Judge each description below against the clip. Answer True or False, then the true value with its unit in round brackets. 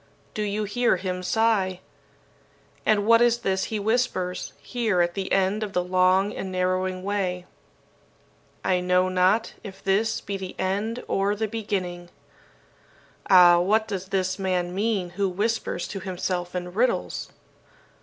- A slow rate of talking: False (145 wpm)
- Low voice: False (190 Hz)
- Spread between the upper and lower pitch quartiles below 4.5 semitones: True (2.5 semitones)